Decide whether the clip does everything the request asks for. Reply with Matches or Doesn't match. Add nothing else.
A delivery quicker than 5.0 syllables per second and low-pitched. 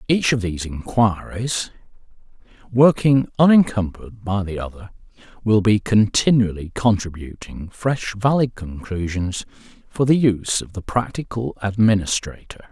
Doesn't match